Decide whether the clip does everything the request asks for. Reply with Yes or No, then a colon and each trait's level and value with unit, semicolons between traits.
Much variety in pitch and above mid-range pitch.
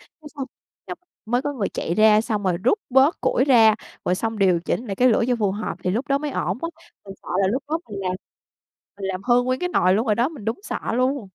No: average, 4.7 semitones; high, 225 Hz